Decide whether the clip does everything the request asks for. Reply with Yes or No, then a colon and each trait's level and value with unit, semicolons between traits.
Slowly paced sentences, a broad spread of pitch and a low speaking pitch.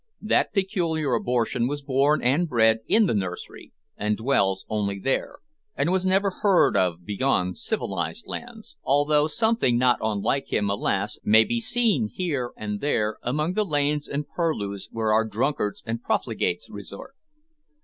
No: average, 150 wpm; wide, 6.8 semitones; low, 125 Hz